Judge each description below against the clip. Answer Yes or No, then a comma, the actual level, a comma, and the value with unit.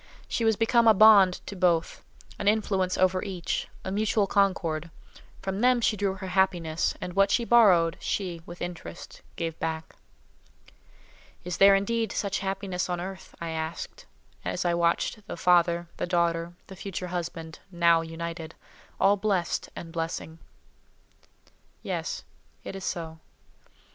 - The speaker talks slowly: No, average, 145 wpm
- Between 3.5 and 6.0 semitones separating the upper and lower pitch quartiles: No, average, 2.8 semitones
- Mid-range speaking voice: Yes, medium, 180 Hz